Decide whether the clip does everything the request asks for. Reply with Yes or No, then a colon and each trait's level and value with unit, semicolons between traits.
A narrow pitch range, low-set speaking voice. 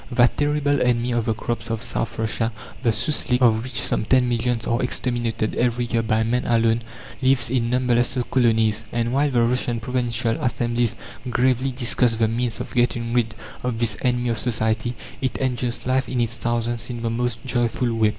Yes: narrow, 1.5 semitones; low, 120 Hz